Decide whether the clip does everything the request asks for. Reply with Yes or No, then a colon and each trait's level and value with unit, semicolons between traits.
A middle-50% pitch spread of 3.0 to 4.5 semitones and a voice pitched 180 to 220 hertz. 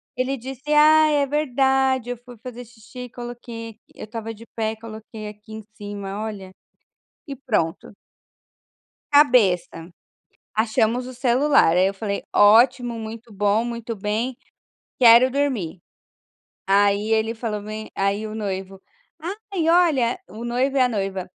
No: average, 3.5 semitones; high, 230 Hz